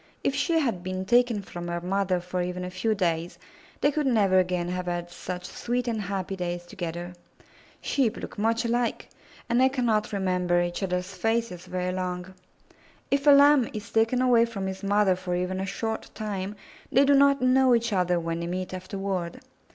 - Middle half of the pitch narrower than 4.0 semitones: No, average, 4.5 semitones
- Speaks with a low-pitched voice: No, high, 195 Hz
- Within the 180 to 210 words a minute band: Yes, average, 190 wpm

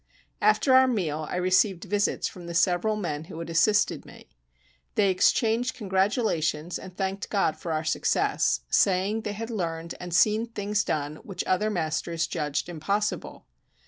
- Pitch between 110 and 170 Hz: No, medium, 185 Hz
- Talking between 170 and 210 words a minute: No, average, 155 wpm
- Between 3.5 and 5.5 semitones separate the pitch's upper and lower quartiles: Yes, average, 4.2 semitones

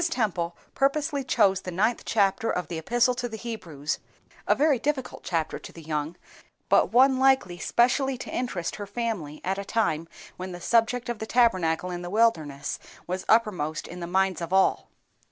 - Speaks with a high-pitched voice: Yes, high, 200 Hz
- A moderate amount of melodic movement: No, wide, 5.7 semitones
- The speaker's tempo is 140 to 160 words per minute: No, average, 180 wpm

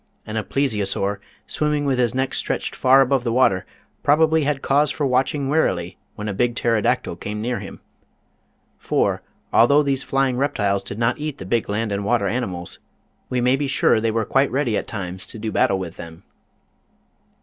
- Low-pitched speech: Yes, low, 120 Hz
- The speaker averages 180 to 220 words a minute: Yes, average, 190 wpm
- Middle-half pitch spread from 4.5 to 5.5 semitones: Yes, average, 4.9 semitones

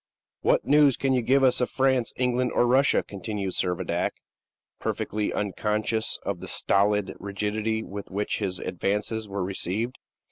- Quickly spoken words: No, average, 145 wpm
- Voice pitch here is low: Yes, low, 105 Hz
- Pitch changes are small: No, average, 3.9 semitones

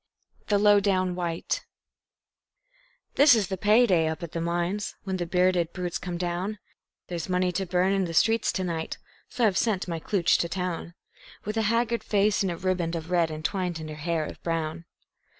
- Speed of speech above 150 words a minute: Yes, average, 195 wpm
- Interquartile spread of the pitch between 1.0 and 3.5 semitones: Yes, average, 2.9 semitones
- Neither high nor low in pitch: Yes, medium, 180 Hz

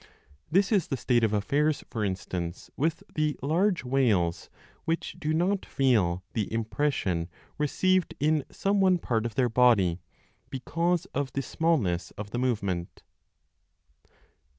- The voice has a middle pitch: No, low, 130 Hz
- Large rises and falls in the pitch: Yes, wide, 7.5 semitones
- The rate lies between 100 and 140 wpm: Yes, slow, 135 wpm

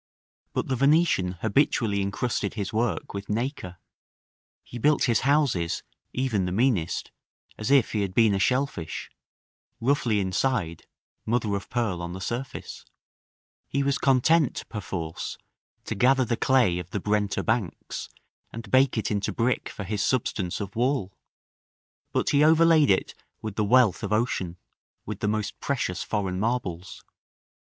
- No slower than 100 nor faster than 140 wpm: No, average, 150 wpm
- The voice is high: No, low, 110 Hz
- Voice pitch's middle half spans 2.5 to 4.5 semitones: No, average, 5.0 semitones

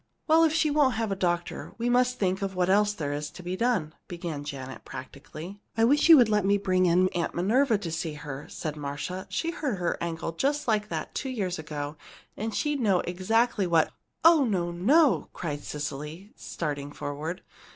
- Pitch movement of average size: No, wide, 6.4 semitones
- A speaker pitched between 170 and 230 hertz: Yes, medium, 185 Hz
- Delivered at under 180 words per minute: No, average, 195 wpm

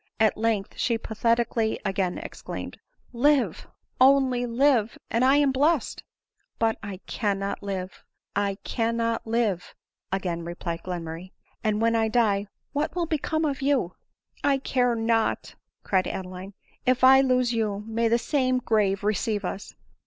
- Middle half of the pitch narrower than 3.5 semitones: No, average, 4.3 semitones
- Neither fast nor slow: Yes, average, 165 wpm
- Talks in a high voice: Yes, high, 225 Hz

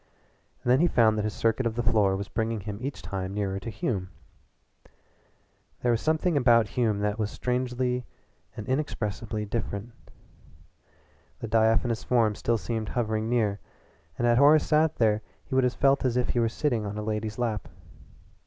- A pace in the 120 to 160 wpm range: No, average, 175 wpm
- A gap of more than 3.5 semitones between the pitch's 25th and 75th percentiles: No, average, 2.8 semitones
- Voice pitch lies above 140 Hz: No, low, 115 Hz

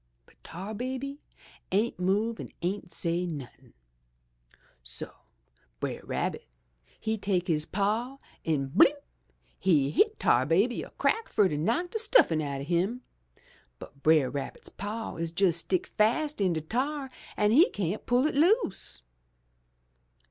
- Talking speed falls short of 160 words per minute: Yes, average, 145 wpm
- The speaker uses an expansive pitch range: Yes, wide, 7.2 semitones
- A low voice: No, high, 200 Hz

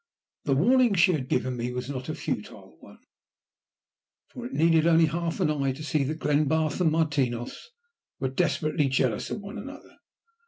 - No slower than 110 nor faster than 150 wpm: No, average, 170 wpm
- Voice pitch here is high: No, medium, 155 Hz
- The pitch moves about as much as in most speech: Yes, average, 4.0 semitones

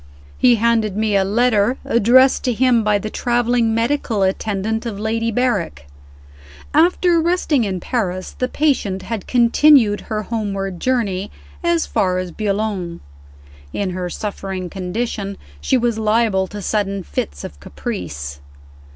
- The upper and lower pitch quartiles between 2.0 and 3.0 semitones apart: No, average, 3.8 semitones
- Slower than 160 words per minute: Yes, slow, 135 wpm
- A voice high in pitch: Yes, high, 215 Hz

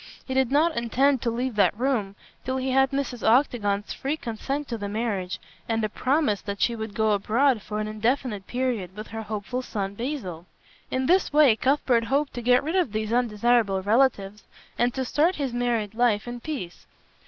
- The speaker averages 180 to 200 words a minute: Yes, average, 190 wpm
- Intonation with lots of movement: No, average, 3.8 semitones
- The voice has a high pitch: Yes, high, 240 Hz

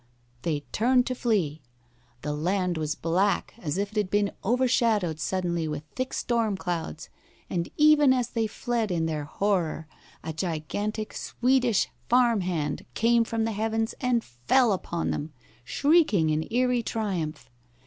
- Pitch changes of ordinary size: No, wide, 6.5 semitones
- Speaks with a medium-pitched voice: No, high, 205 Hz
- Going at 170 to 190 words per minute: No, average, 150 wpm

